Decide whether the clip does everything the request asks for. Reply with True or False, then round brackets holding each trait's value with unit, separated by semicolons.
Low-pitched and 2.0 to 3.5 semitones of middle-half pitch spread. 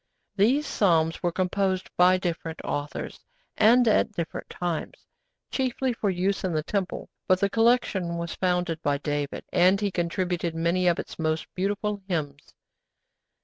False (180 Hz; 3.1 semitones)